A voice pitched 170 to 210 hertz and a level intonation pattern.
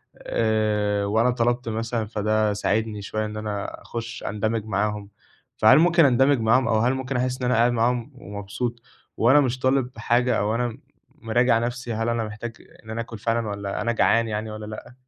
No: low, 115 Hz; narrow, 2.2 semitones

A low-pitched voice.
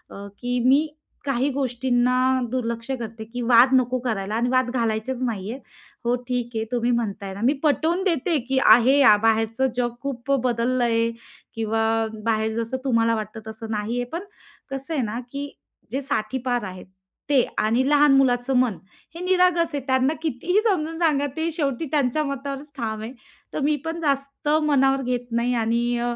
No: very high, 250 Hz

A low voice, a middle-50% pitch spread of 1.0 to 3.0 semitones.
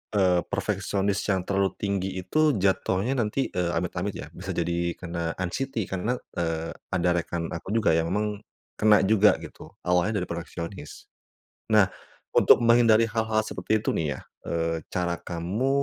No: very low, 95 Hz; average, 3.5 semitones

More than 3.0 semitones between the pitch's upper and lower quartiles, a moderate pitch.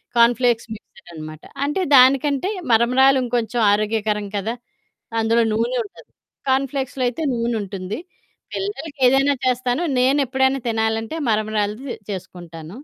No: average, 3.7 semitones; high, 235 Hz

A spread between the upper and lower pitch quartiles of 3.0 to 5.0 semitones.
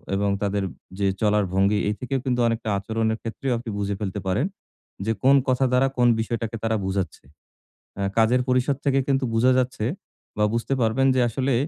Yes: average, 3.7 semitones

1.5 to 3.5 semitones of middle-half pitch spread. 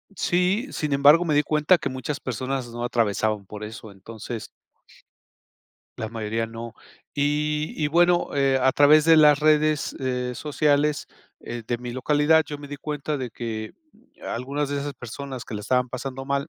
No: average, 3.9 semitones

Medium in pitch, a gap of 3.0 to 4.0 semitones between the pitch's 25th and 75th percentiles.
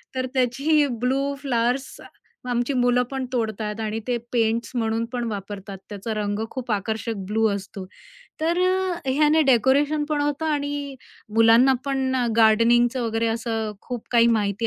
No: high, 240 Hz; average, 3.5 semitones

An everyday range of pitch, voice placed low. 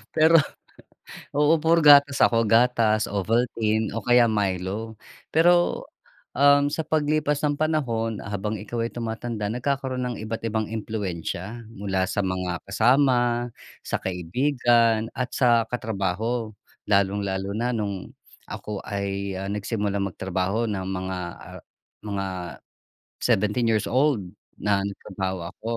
Yes: average, 3.9 semitones; low, 110 Hz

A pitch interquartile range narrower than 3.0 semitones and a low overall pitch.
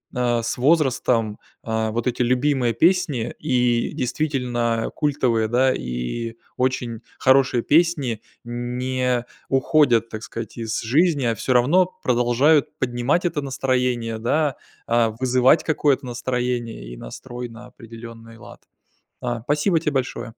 Yes: narrow, 2.5 semitones; low, 125 Hz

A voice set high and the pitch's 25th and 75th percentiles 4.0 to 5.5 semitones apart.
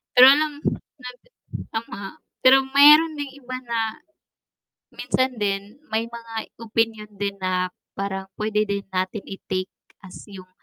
Yes: high, 220 Hz; average, 4.4 semitones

